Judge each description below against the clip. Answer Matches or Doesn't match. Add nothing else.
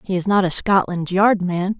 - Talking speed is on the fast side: Matches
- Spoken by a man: Doesn't match